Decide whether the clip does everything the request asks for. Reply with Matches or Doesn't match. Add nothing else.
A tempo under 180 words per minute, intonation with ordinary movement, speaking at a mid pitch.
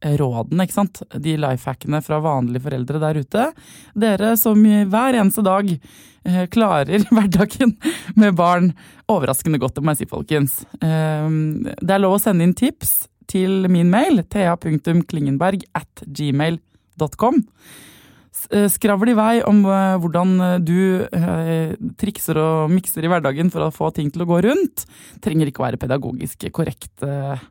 Matches